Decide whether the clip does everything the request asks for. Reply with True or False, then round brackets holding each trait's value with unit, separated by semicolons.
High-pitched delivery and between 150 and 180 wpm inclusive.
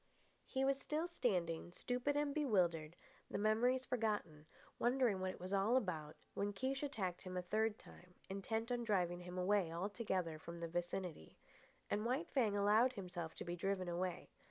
True (200 Hz; 170 wpm)